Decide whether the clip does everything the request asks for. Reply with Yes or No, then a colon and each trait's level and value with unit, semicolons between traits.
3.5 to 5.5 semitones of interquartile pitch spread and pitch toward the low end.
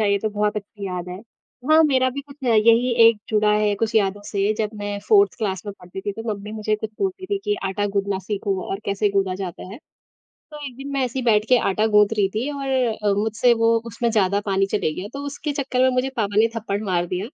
No: average, 3.9 semitones; high, 215 Hz